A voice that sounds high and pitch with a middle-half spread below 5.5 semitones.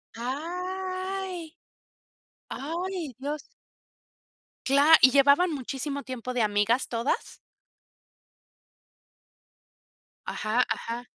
No: very high, 280 Hz; wide, 6.1 semitones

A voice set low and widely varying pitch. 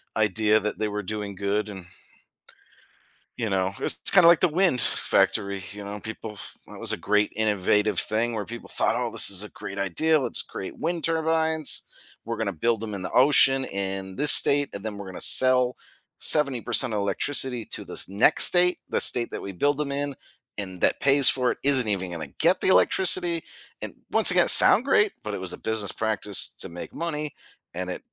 Yes: low, 110 Hz; wide, 5.9 semitones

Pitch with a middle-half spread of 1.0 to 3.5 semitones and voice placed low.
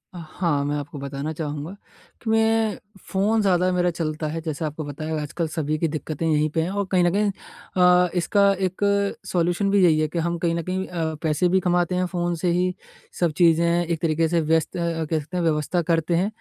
No: average, 2.8 semitones; medium, 170 Hz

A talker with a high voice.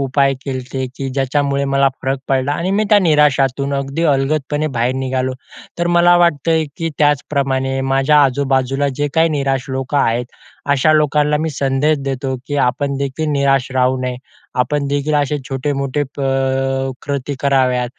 No: medium, 140 Hz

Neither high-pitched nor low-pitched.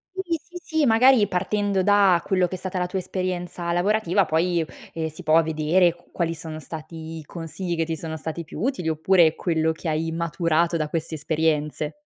Yes: medium, 170 Hz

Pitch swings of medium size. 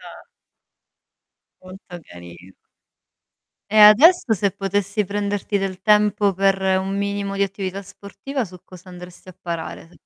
No: narrow, 1.9 semitones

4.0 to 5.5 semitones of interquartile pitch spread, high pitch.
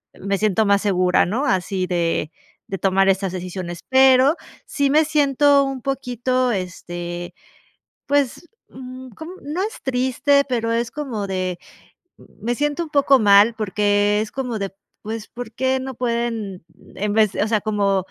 Yes: average, 5.2 semitones; high, 225 Hz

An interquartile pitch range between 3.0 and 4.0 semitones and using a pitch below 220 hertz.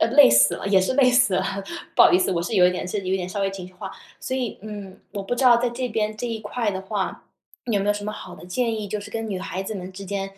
Yes: average, 3.3 semitones; high, 205 Hz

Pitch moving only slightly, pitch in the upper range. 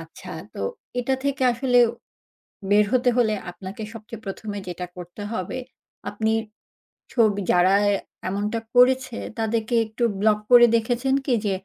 No: average, 3.2 semitones; high, 220 Hz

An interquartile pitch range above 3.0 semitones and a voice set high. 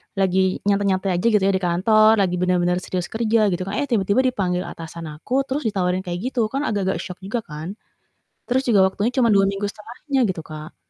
Yes: average, 3.6 semitones; high, 195 Hz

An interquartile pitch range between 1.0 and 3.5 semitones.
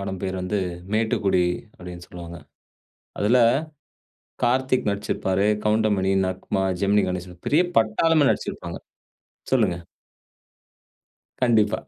Yes: average, 3.1 semitones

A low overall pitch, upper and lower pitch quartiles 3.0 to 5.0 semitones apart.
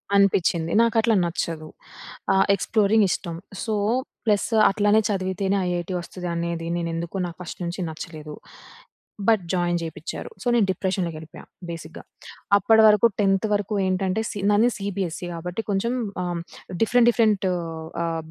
No: high, 190 Hz; average, 3.5 semitones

